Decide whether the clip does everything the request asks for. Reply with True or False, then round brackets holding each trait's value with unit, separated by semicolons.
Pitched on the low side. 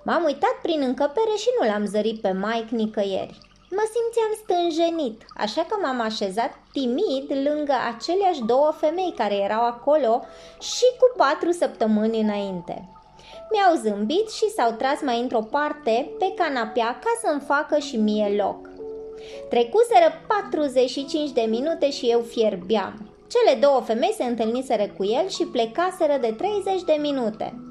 False (280 Hz)